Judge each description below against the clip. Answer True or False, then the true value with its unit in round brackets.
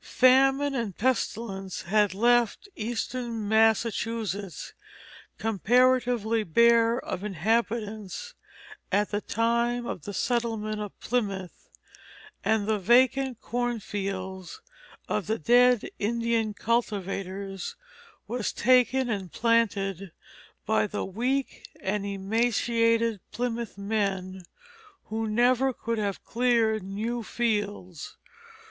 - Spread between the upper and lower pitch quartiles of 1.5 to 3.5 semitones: True (3.1 semitones)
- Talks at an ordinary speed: False (95 wpm)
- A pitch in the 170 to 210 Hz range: False (220 Hz)